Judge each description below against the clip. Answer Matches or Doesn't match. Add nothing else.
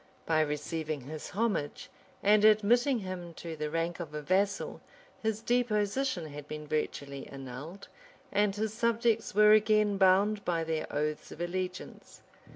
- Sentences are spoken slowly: Doesn't match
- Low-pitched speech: Doesn't match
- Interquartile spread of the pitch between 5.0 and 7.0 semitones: Matches